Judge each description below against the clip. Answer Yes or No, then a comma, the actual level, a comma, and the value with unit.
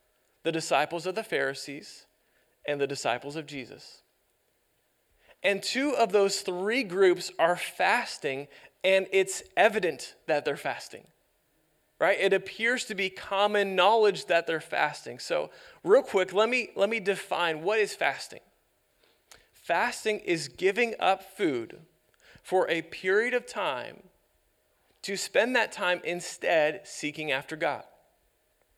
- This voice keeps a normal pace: No, slow, 130 wpm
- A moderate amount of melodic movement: Yes, average, 4.0 semitones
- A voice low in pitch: No, high, 190 Hz